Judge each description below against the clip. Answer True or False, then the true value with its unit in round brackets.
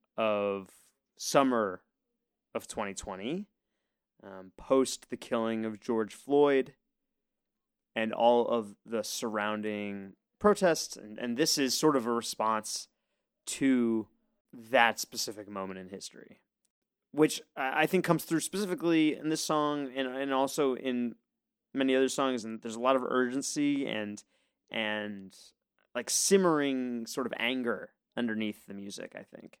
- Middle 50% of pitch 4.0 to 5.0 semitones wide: False (5.6 semitones)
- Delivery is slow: True (130 wpm)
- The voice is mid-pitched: False (125 Hz)